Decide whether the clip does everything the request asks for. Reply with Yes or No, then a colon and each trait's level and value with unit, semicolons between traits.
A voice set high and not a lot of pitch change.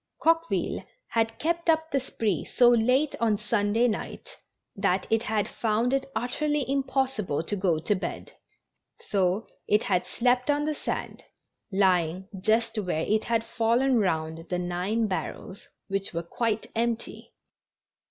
No: high, 225 Hz; average, 4.7 semitones